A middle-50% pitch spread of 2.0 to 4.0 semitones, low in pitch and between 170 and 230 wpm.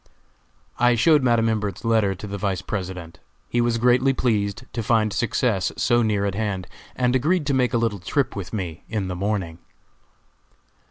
Yes: average, 3.6 semitones; low, 110 Hz; average, 175 wpm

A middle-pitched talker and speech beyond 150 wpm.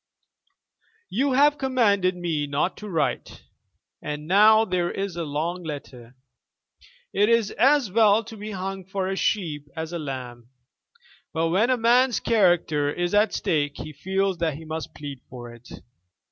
Yes: medium, 180 Hz; average, 160 wpm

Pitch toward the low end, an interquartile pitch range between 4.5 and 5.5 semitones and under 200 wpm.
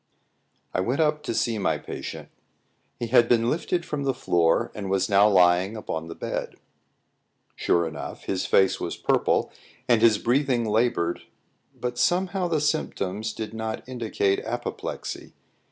Yes: low, 110 Hz; average, 5.0 semitones; average, 150 wpm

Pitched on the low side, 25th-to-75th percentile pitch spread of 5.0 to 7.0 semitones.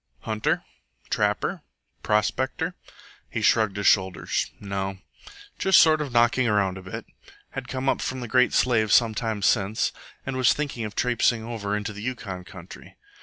No: low, 110 Hz; average, 3.9 semitones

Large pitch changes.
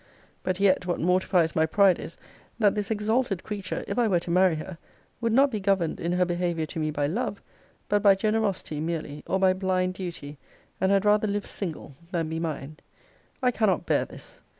No: average, 3.7 semitones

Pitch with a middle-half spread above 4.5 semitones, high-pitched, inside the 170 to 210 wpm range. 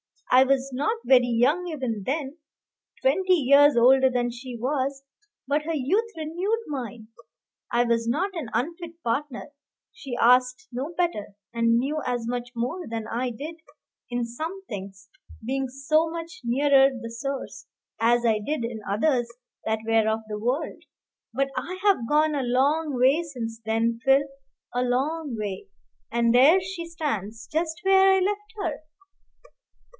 No: average, 5.1 semitones; very high, 265 Hz; average, 155 wpm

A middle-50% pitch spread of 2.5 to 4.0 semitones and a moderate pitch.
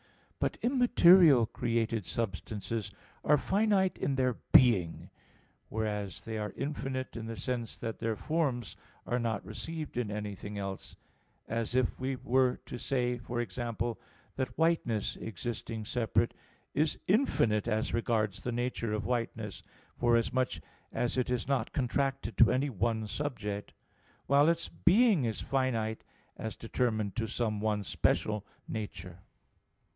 No: average, 3.4 semitones; low, 120 Hz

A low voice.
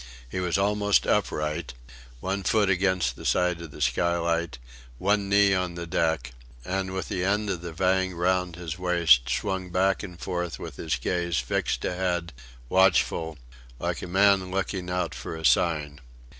Yes: very low, 90 Hz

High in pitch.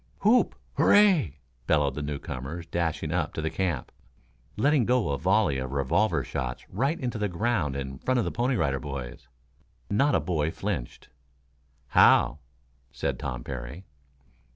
No: very low, 80 Hz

